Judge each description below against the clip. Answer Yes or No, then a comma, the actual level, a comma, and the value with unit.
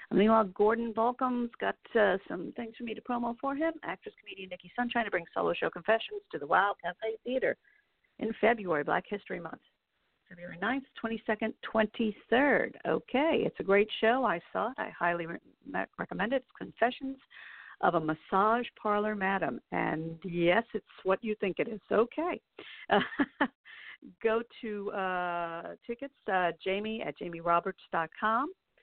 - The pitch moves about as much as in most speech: Yes, average, 4.5 semitones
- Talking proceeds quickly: No, average, 160 wpm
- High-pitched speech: Yes, high, 220 Hz